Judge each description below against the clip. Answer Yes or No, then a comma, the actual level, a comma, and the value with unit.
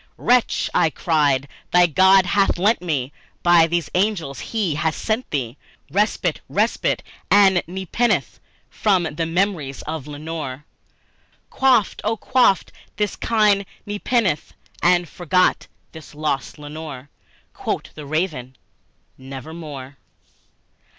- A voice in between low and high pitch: Yes, medium, 170 Hz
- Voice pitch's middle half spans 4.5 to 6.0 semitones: Yes, average, 5.1 semitones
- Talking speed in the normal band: No, slow, 110 wpm